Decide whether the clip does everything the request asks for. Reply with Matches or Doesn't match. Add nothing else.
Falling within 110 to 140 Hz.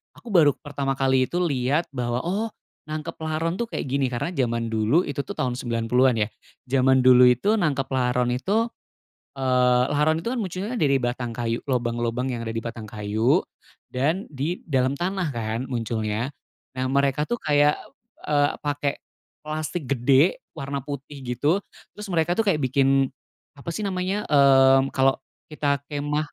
Matches